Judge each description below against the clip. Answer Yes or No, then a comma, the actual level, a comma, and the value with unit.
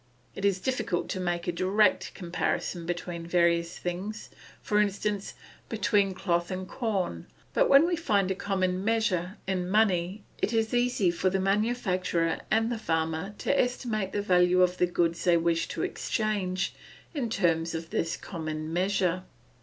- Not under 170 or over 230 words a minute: No, average, 160 wpm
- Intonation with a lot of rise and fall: No, average, 3.4 semitones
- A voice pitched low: No, medium, 185 Hz